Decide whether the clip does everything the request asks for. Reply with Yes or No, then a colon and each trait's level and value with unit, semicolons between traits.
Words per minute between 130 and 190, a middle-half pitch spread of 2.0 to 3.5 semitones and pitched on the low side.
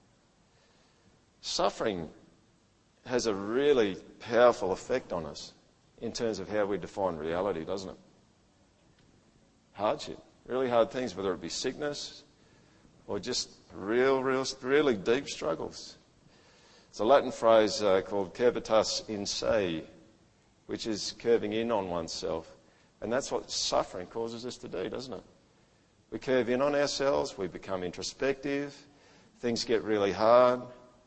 No: slow, 135 wpm; average, 3.9 semitones; low, 120 Hz